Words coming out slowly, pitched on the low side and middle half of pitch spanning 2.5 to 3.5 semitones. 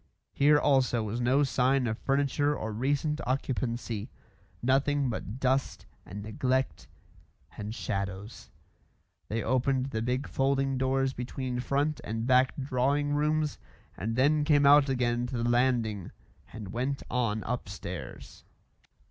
Yes: slow, 130 wpm; low, 130 Hz; average, 2.8 semitones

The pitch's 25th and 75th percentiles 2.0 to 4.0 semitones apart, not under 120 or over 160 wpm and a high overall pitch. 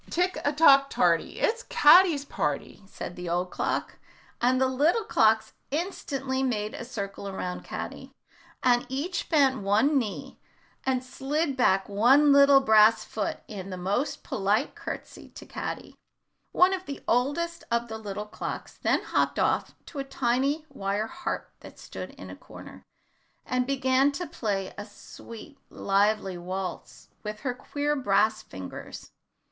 No: wide, 5.6 semitones; average, 150 wpm; very high, 250 Hz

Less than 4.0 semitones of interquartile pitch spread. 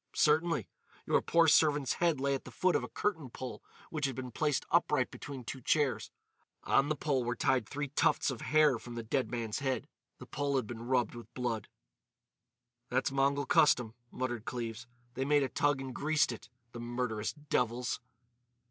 Yes: average, 3.3 semitones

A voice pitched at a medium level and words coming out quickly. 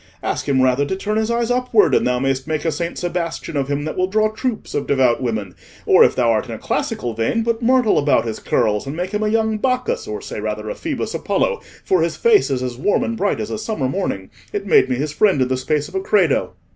Yes: medium, 175 Hz; fast, 260 wpm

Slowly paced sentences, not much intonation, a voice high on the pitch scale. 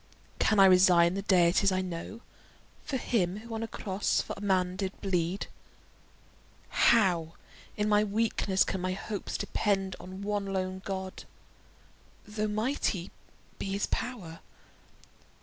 Yes: slow, 130 wpm; narrow, 2.2 semitones; high, 195 Hz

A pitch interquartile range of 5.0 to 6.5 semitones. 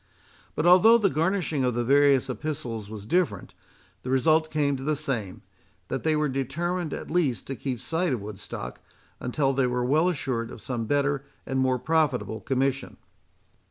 No: average, 4.0 semitones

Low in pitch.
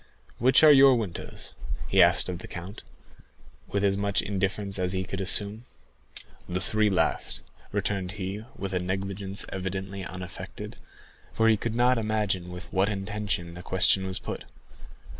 Yes: low, 100 Hz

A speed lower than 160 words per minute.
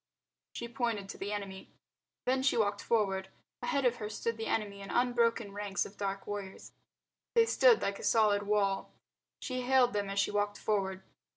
No: average, 180 wpm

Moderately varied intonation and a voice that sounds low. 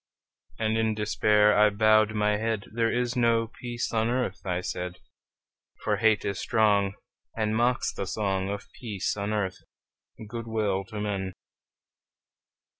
No: narrow, 1.9 semitones; low, 105 Hz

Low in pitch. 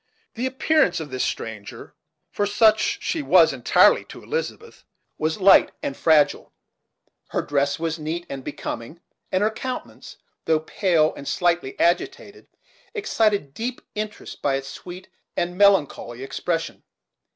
No: medium, 175 Hz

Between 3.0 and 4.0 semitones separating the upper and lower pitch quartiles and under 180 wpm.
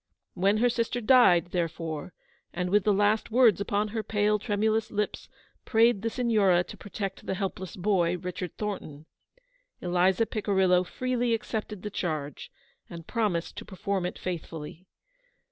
Yes: average, 3.4 semitones; average, 145 wpm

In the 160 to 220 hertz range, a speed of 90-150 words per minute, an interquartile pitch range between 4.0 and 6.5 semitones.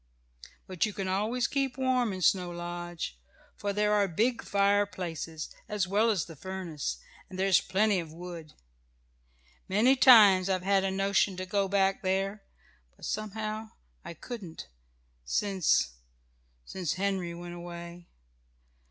No: high, 190 Hz; average, 140 wpm; average, 3.1 semitones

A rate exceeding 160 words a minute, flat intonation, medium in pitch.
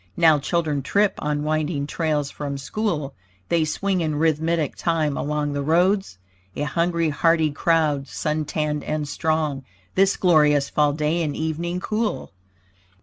No: average, 140 wpm; narrow, 2.3 semitones; medium, 155 Hz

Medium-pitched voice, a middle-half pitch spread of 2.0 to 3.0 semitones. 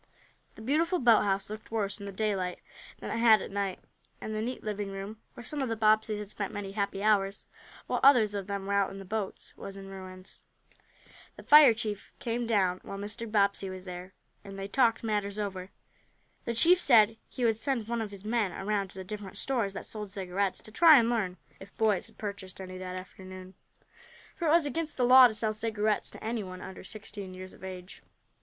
No: high, 205 Hz; average, 2.7 semitones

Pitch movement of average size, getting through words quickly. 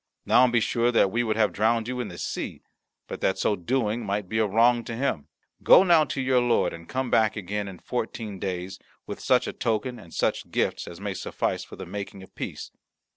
Yes: average, 3.7 semitones; fast, 220 wpm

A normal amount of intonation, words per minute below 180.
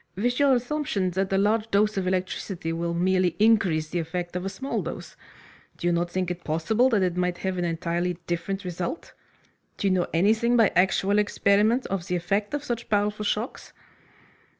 No: average, 3.3 semitones; average, 190 wpm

